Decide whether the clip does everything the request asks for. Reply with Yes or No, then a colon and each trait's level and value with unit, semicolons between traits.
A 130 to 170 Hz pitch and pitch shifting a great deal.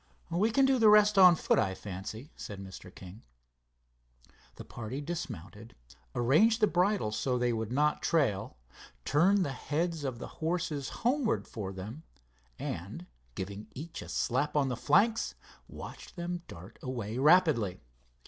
Yes: medium, 140 Hz; wide, 8.6 semitones